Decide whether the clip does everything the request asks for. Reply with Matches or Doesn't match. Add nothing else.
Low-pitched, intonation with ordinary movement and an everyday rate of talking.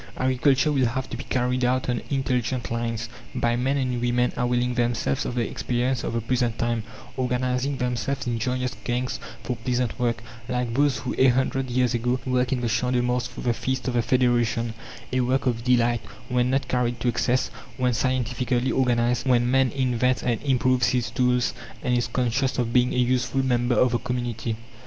Doesn't match